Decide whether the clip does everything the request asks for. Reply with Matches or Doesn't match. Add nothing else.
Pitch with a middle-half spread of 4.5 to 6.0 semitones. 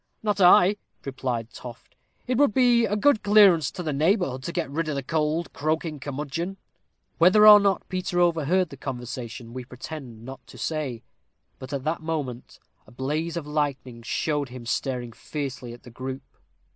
Matches